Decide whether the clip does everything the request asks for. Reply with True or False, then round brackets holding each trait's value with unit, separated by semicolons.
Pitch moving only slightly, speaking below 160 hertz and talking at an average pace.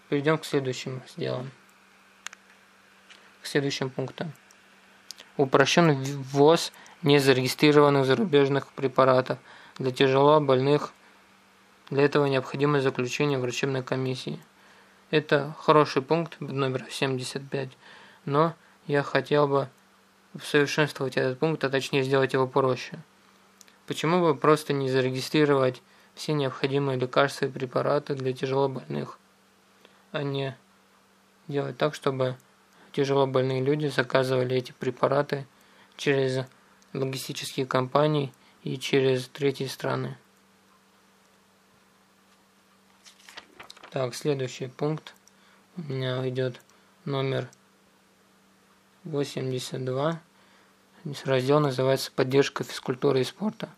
False (2.0 semitones; 140 Hz; 90 wpm)